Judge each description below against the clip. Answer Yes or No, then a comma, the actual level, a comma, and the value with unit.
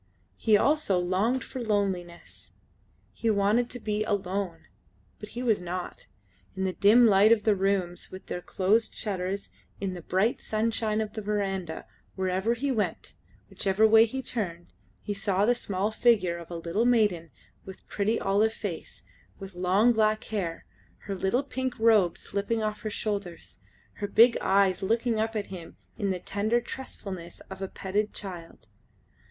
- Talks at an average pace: Yes, average, 160 wpm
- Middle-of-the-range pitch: No, high, 205 Hz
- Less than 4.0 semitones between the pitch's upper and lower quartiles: Yes, average, 2.9 semitones